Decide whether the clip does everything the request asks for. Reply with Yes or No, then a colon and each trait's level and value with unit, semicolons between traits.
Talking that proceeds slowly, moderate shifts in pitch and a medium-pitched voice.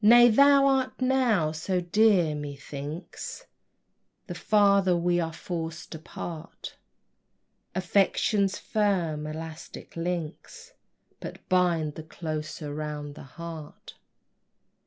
Yes: slow, 95 wpm; average, 4.4 semitones; medium, 170 Hz